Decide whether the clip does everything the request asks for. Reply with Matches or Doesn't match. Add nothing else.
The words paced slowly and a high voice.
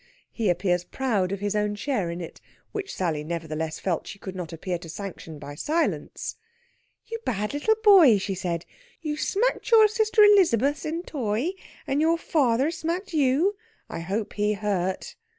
Doesn't match